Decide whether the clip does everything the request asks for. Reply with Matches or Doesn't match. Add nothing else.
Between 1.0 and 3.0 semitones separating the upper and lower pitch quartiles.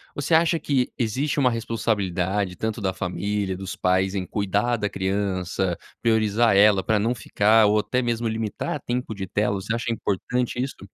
Doesn't match